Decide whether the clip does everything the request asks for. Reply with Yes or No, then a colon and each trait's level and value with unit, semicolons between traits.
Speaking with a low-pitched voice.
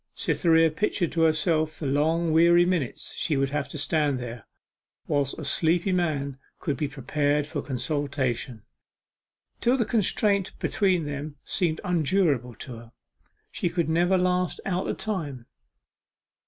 No: medium, 155 Hz